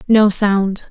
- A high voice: Yes, high, 205 Hz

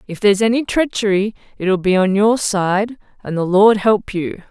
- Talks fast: No, average, 185 wpm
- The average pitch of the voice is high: Yes, high, 200 Hz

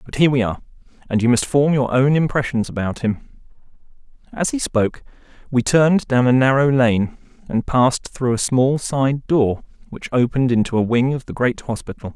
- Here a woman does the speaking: No, male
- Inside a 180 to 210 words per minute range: Yes, average, 190 wpm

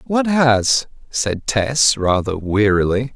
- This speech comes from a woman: No, male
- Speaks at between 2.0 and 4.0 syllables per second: Yes, 3.2 syllables/s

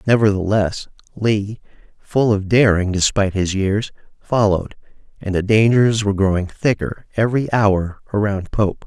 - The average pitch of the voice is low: Yes, low, 105 Hz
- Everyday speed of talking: No, slow, 130 wpm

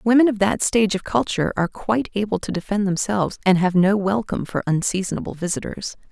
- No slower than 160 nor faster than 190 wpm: Yes, average, 185 wpm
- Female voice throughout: Yes, female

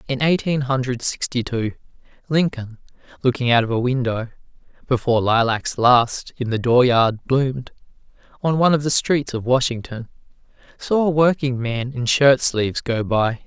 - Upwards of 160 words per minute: No, average, 145 wpm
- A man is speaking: Yes, male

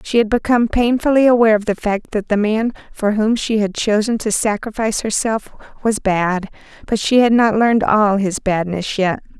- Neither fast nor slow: Yes, average, 190 wpm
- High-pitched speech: Yes, high, 215 Hz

